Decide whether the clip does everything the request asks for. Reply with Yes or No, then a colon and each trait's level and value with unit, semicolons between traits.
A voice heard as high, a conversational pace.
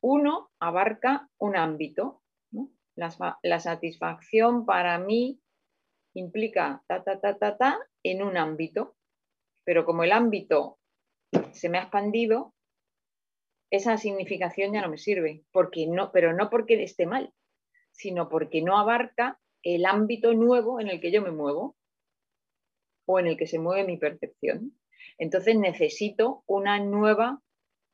Yes: high, 200 Hz; average, 140 wpm